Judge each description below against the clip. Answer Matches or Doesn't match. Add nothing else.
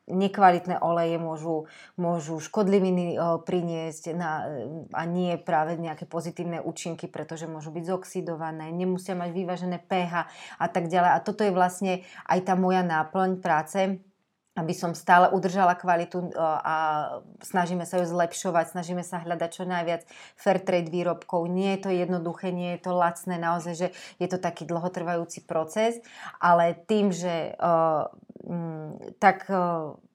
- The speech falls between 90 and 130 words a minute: Doesn't match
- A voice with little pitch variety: Matches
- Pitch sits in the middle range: Matches